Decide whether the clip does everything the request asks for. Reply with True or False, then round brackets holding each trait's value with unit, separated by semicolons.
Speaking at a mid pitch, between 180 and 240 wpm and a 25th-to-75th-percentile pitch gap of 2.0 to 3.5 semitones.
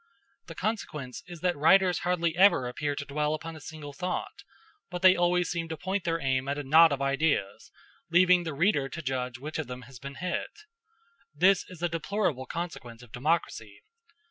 False (160 Hz; 190 wpm; 4.4 semitones)